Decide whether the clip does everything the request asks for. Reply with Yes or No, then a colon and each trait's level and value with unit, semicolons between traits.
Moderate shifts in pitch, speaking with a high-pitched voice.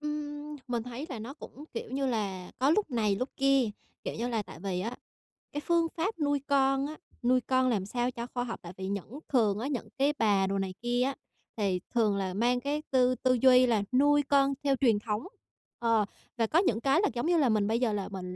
Yes: average, 4.5 semitones; high, 245 Hz